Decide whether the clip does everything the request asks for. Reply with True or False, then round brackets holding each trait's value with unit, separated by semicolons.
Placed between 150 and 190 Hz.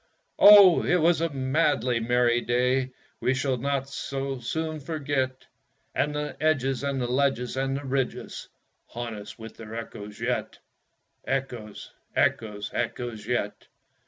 False (130 Hz)